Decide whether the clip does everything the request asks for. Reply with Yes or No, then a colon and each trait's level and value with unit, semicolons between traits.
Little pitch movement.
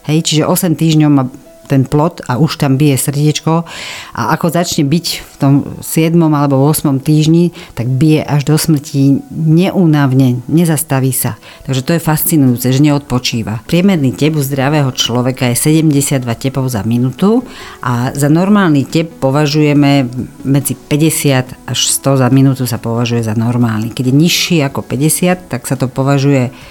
No: average, 3.4 semitones